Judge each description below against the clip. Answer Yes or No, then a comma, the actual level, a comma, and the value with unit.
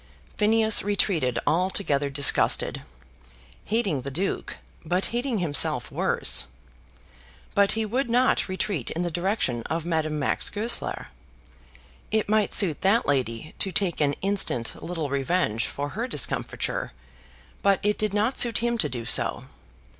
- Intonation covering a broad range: Yes, wide, 6.8 semitones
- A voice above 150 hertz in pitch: Yes, medium, 185 Hz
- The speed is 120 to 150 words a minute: Yes, average, 140 wpm